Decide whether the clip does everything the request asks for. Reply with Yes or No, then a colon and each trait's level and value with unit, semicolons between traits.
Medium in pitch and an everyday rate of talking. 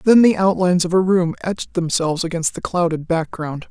Yes: medium, 175 Hz; average, 195 wpm